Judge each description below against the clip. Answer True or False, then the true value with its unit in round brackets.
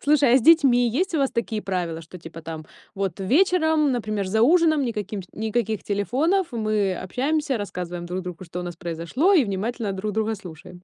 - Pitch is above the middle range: True (215 Hz)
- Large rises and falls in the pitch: True (6.9 semitones)